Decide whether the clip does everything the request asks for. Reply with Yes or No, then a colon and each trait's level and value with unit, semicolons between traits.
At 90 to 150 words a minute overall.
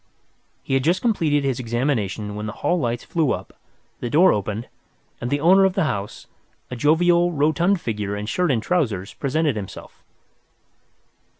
No: average, 165 wpm